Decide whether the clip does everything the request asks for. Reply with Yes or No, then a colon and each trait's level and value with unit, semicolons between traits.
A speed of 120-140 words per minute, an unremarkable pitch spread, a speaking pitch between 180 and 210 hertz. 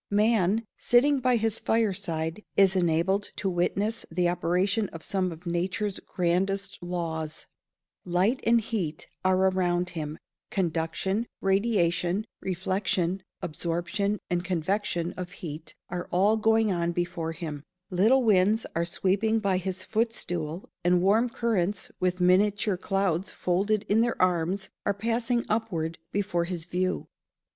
Yes: slow, 135 wpm; average, 3.2 semitones; medium, 185 Hz